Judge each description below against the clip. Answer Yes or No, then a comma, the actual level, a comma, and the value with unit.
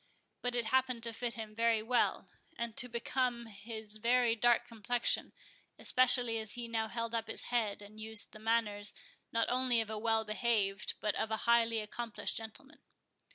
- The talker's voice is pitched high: Yes, high, 230 Hz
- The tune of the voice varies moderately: No, narrow, 1.6 semitones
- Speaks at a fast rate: No, average, 175 wpm